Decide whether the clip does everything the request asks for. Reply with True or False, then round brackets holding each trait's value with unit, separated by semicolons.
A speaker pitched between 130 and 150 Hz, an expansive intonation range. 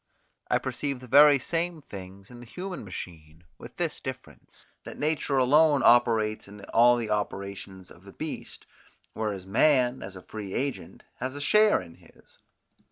False (120 Hz; 6.5 semitones)